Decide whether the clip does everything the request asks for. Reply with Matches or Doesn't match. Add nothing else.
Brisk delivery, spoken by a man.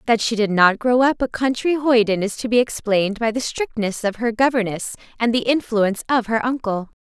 Doesn't match